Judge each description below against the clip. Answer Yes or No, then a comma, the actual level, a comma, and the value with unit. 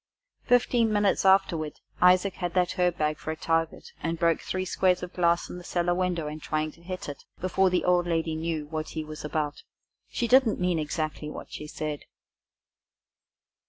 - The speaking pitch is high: No, medium, 170 Hz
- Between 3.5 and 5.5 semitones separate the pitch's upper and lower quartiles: No, average, 2.8 semitones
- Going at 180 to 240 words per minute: Yes, average, 185 wpm